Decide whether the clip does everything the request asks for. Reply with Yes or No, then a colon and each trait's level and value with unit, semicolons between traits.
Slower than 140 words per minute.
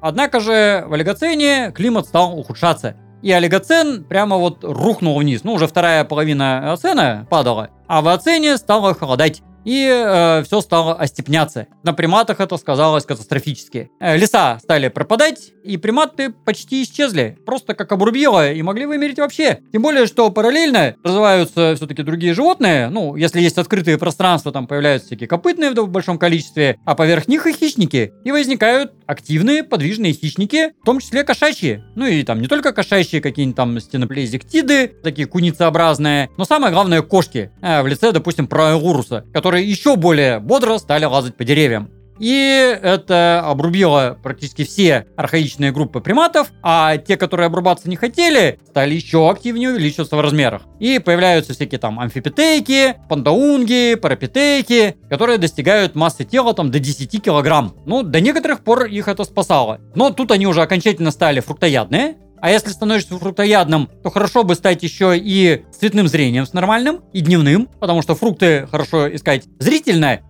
No: average, 155 wpm